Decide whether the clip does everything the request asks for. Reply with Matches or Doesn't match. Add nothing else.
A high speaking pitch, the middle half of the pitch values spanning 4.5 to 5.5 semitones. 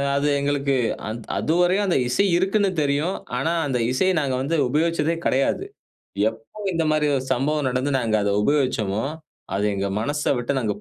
Doesn't match